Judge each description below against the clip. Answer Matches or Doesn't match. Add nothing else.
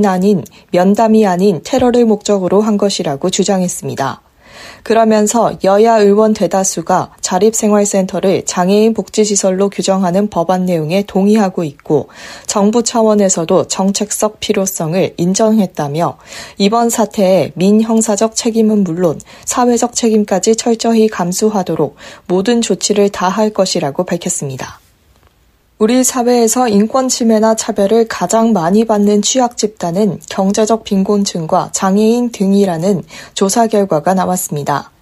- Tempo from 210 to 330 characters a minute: Matches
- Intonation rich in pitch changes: Doesn't match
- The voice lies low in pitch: Doesn't match